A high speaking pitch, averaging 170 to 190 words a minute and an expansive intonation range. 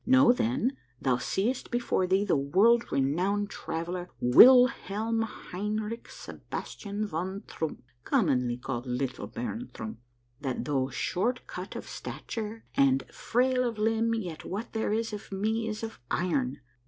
No: high, 205 Hz; average, 140 wpm; wide, 6.6 semitones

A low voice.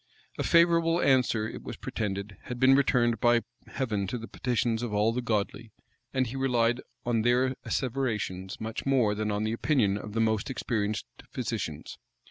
Yes: low, 115 Hz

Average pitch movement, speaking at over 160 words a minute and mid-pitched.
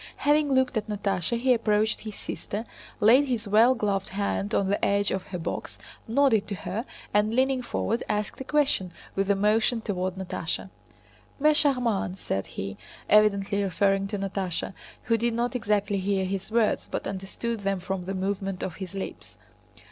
No: average, 3.1 semitones; average, 170 wpm; high, 205 Hz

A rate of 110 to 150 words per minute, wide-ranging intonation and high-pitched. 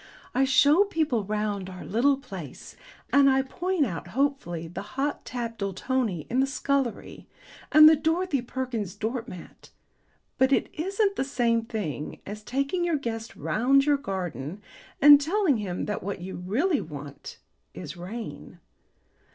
Yes: average, 145 wpm; wide, 6.0 semitones; high, 245 Hz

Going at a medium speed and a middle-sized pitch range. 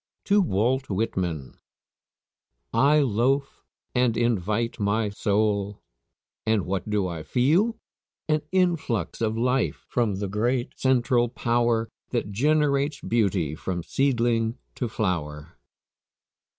No: slow, 110 wpm; average, 4.6 semitones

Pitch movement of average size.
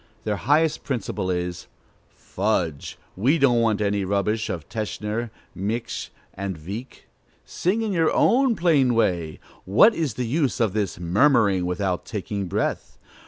No: wide, 5.8 semitones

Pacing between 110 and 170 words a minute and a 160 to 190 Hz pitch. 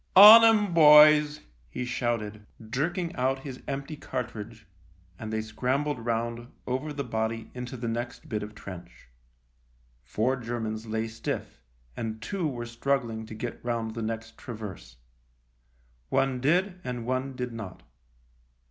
No: average, 145 wpm; low, 120 Hz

